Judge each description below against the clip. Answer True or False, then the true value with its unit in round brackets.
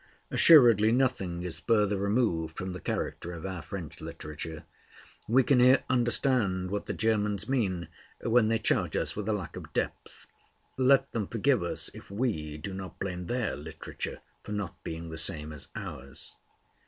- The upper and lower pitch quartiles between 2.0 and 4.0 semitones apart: False (5.5 semitones)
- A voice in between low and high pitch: False (100 Hz)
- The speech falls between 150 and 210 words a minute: True (165 wpm)